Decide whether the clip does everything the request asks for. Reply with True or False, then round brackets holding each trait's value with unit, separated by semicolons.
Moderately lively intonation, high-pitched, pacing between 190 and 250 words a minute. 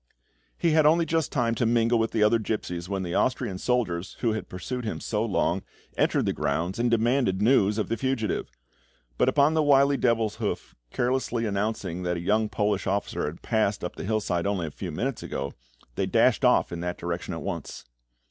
False (4.8 semitones; 110 Hz; 195 wpm)